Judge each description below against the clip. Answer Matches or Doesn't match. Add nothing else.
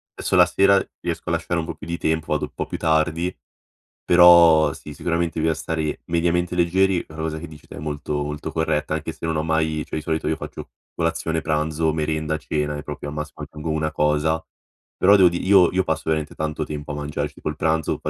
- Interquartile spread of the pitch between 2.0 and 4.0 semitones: Doesn't match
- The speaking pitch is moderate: Doesn't match